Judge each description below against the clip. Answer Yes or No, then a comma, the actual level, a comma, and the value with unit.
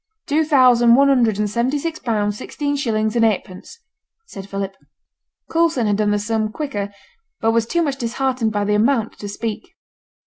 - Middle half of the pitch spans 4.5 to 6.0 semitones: Yes, average, 4.8 semitones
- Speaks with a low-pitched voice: No, high, 230 Hz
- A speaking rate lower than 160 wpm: No, average, 175 wpm